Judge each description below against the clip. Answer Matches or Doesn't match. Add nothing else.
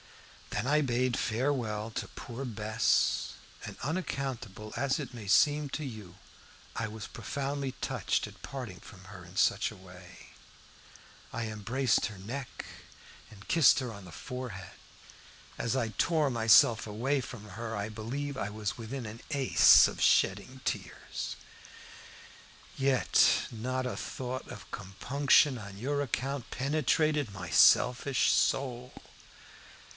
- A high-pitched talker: Doesn't match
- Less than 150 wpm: Matches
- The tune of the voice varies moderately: Matches